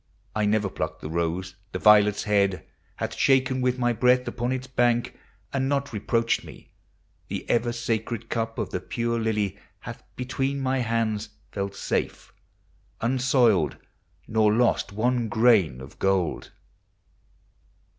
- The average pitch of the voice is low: Yes, low, 115 Hz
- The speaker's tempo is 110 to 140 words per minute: Yes, slow, 135 wpm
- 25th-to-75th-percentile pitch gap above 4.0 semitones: No, average, 3.3 semitones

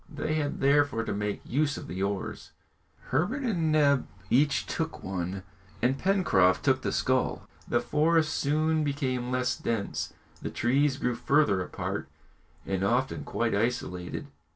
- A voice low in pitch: Yes, low, 130 Hz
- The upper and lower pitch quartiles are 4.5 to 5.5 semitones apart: Yes, average, 5.0 semitones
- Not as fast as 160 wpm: Yes, average, 145 wpm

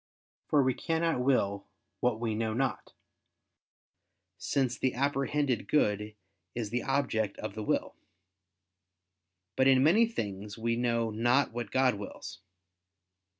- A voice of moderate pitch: No, low, 120 Hz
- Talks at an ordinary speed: No, slow, 125 wpm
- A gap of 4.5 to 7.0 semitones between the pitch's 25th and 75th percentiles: No, average, 3.8 semitones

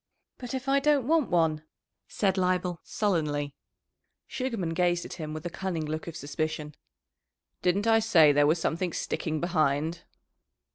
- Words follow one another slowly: No, average, 150 wpm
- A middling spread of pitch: Yes, average, 4.4 semitones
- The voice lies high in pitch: No, medium, 175 Hz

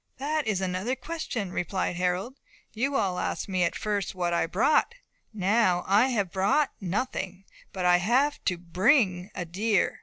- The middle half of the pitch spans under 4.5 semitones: No, average, 4.9 semitones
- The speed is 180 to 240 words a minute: No, average, 170 wpm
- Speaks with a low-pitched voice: No, high, 195 Hz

